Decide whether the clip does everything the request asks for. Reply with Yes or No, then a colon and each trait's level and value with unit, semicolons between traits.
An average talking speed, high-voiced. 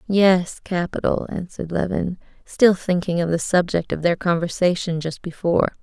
No: average, 145 wpm; medium, 175 Hz